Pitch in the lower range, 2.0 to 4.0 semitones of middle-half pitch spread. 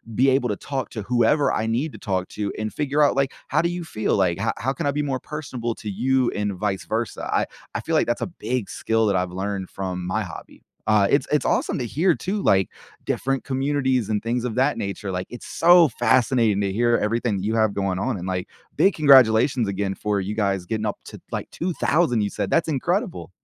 No: low, 115 Hz; average, 5.3 semitones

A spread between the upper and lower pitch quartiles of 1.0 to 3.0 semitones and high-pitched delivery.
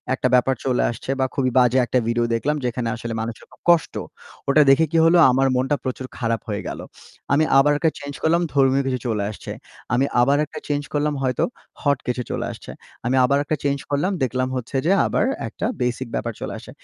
No: average, 2.7 semitones; low, 130 Hz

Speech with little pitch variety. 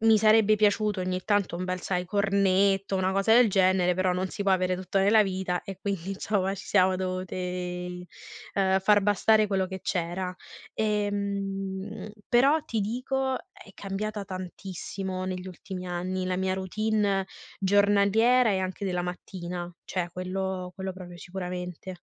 Yes: narrow, 1.8 semitones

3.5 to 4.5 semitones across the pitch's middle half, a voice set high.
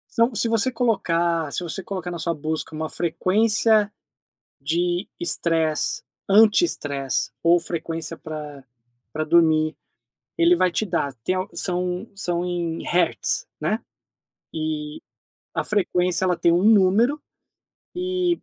No: average, 4.1 semitones; medium, 175 Hz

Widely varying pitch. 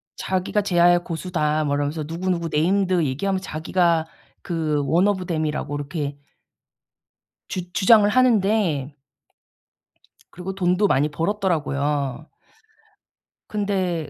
No: average, 4.0 semitones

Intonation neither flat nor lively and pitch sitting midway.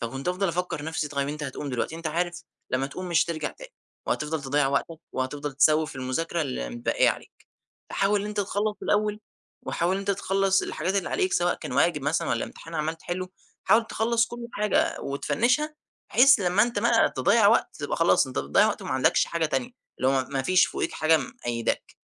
No: wide, 5.8 semitones; medium, 170 Hz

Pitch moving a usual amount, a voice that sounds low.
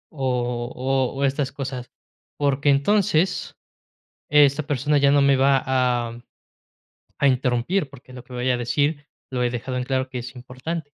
No: narrow, 2.3 semitones; low, 130 Hz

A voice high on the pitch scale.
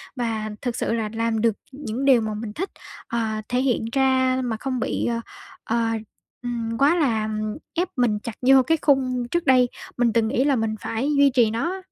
Yes: high, 240 Hz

